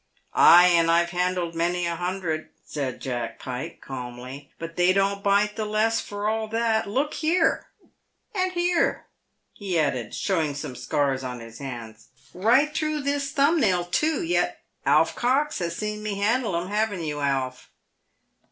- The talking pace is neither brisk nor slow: Yes, average, 165 wpm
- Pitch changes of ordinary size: No, wide, 7.2 semitones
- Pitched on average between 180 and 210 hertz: Yes, medium, 185 Hz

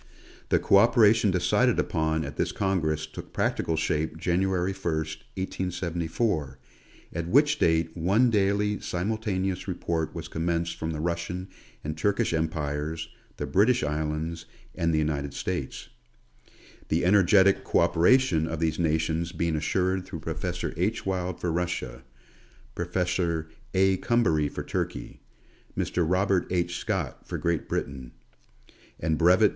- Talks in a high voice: No, very low, 85 Hz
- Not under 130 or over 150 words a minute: Yes, slow, 135 wpm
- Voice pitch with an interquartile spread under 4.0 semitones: Yes, average, 3.1 semitones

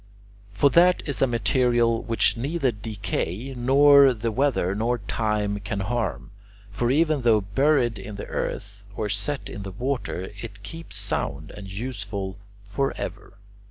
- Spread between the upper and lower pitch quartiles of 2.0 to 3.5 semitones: No, average, 4.8 semitones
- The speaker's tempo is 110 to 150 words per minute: Yes, average, 145 wpm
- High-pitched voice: No, low, 115 Hz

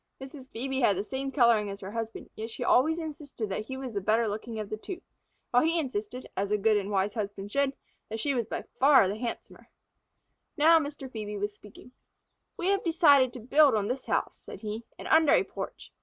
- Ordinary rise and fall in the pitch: Yes, average, 4.7 semitones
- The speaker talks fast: Yes, fast, 215 wpm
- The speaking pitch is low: No, high, 235 Hz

